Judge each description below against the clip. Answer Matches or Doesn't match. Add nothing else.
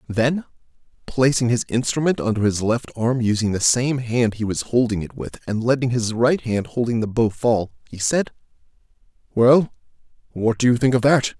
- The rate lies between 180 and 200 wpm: Matches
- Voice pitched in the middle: Doesn't match